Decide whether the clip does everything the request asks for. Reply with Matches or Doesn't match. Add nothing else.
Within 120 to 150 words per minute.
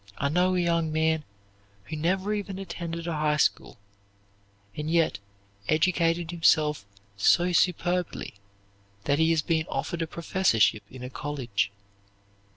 Matches